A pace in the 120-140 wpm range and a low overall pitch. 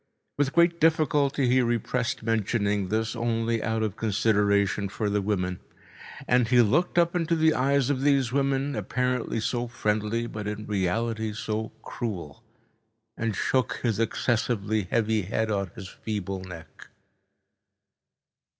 Yes: slow, 135 wpm; low, 115 Hz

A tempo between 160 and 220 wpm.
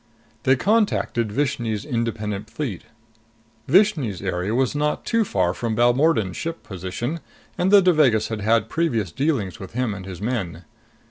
No: average, 145 wpm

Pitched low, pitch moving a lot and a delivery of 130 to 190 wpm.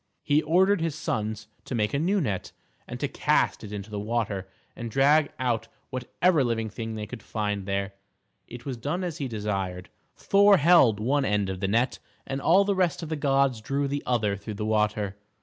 No: low, 120 Hz; wide, 5.7 semitones; average, 200 wpm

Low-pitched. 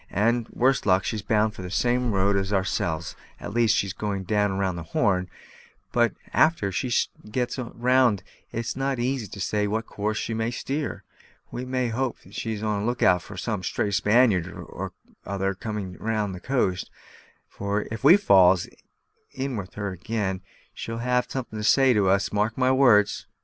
Yes: low, 105 Hz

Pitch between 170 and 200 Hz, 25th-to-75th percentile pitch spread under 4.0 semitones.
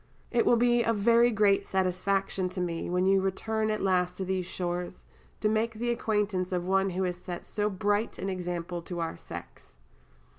Yes: high, 190 Hz; average, 3.0 semitones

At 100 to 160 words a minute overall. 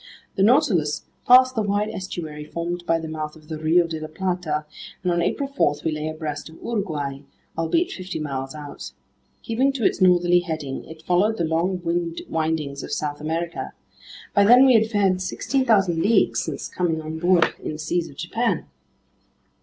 No: average, 175 wpm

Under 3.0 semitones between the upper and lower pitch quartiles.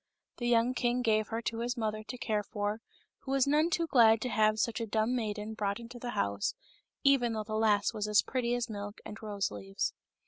Yes: narrow, 2.4 semitones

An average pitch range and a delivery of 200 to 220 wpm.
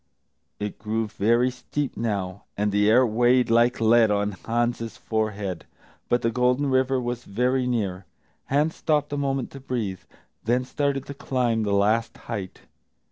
No: average, 3.2 semitones; average, 155 wpm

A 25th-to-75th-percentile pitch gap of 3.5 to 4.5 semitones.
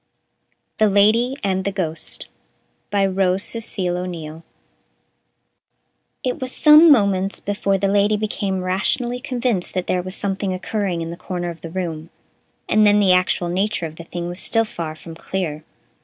No: average, 2.9 semitones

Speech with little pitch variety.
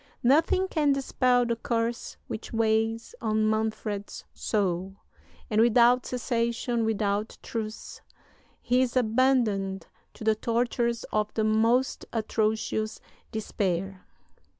Yes: narrow, 2.0 semitones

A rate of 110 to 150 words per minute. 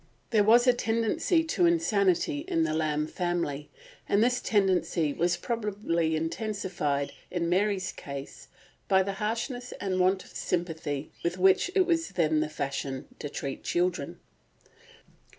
Yes: average, 140 wpm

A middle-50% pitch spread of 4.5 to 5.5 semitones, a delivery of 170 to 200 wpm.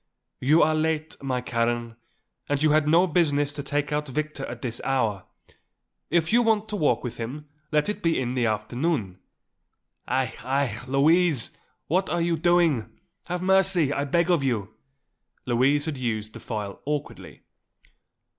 No: average, 5.0 semitones; average, 160 wpm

